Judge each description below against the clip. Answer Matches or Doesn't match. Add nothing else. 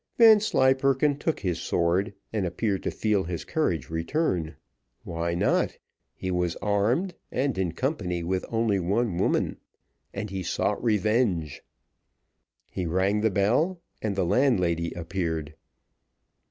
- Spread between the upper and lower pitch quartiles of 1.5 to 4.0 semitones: Doesn't match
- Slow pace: Matches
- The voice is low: Matches